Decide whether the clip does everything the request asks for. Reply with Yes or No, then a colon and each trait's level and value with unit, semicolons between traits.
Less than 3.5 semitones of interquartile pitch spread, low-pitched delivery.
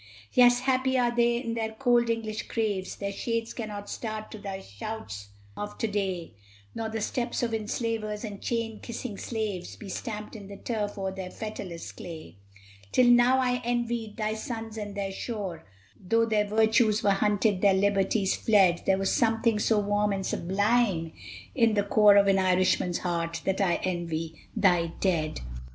No: average, 3.0 semitones; high, 210 Hz